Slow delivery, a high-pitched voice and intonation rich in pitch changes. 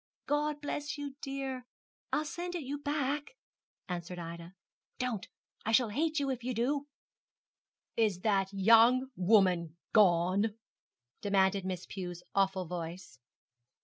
Yes: slow, 125 wpm; high, 220 Hz; wide, 6.9 semitones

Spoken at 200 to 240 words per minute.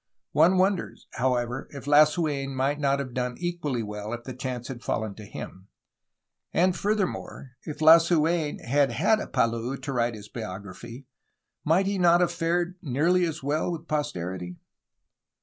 No: average, 160 wpm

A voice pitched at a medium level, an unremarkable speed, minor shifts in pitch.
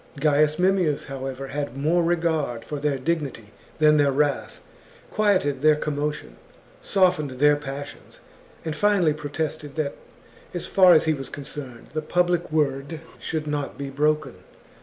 Yes: medium, 150 Hz; average, 150 wpm; narrow, 2.3 semitones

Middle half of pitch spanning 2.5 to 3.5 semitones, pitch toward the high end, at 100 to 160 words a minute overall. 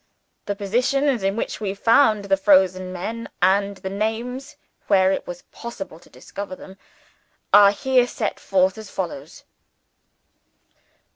Yes: average, 3.2 semitones; high, 200 Hz; slow, 135 wpm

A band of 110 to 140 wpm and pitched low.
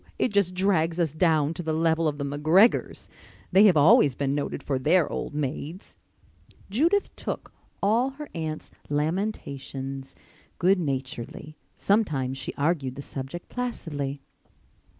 No: slow, 135 wpm; medium, 155 Hz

